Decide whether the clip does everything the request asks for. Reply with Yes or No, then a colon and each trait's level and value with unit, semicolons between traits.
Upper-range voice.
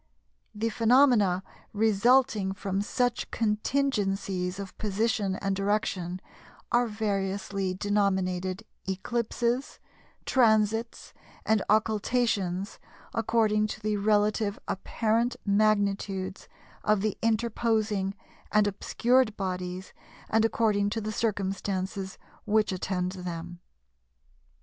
Yes: high, 205 Hz